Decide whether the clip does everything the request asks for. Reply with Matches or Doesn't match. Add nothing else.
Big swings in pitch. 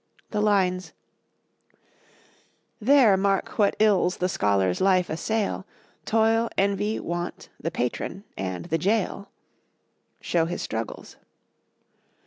Doesn't match